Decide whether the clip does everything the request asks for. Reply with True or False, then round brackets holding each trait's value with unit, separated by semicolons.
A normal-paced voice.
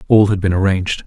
False (225 wpm)